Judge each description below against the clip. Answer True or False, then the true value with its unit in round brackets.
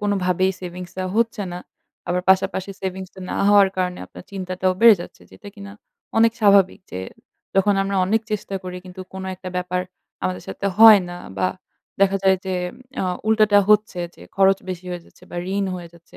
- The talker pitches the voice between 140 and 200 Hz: True (190 Hz)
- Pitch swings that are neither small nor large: False (1.9 semitones)